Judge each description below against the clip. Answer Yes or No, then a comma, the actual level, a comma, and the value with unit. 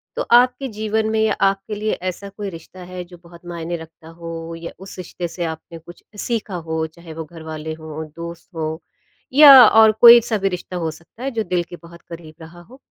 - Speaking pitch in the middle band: Yes, medium, 175 Hz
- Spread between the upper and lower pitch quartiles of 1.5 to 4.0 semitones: No, average, 4.6 semitones